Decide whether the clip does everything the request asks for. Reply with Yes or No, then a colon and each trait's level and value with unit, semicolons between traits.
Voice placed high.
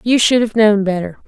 Yes: high, 215 Hz